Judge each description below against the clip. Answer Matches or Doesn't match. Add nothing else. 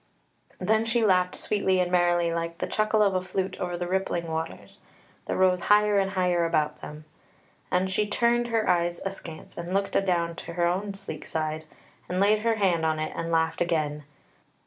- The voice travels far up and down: Doesn't match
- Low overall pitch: Doesn't match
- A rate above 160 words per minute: Matches